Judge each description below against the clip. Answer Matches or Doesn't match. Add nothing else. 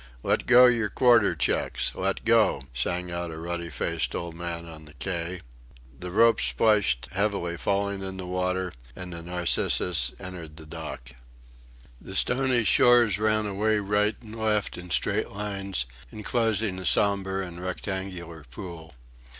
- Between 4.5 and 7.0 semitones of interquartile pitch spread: Doesn't match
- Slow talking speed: Doesn't match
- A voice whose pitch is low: Matches